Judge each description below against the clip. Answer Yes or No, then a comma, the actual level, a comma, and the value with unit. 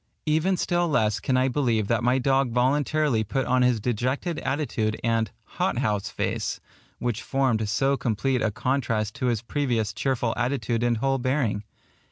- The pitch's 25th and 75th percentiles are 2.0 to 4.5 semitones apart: Yes, average, 3.4 semitones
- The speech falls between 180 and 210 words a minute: No, average, 165 wpm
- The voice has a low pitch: Yes, low, 125 Hz